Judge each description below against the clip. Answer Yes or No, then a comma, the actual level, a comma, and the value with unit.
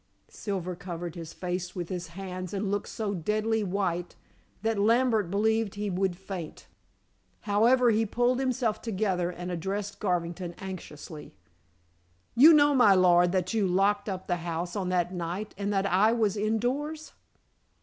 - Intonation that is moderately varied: Yes, average, 3.5 semitones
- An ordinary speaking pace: Yes, average, 150 wpm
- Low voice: No, high, 195 Hz